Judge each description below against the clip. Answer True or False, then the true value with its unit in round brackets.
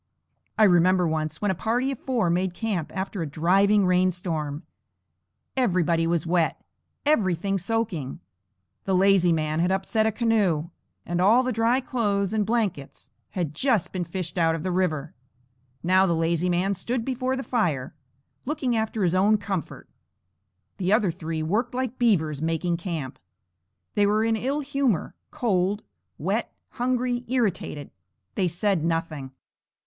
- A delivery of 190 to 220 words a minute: False (150 wpm)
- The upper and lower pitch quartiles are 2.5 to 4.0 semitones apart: False (5.0 semitones)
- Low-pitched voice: False (190 Hz)